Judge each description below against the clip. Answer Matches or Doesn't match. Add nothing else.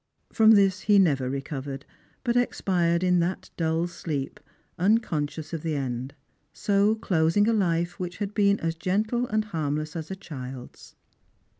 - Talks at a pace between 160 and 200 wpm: Doesn't match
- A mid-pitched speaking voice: Matches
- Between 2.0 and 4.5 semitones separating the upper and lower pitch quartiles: Doesn't match